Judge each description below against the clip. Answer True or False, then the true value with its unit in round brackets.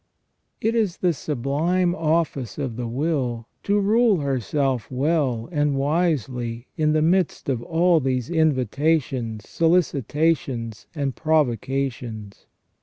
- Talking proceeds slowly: True (115 wpm)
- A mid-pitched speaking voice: True (145 Hz)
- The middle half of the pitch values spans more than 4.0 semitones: True (4.8 semitones)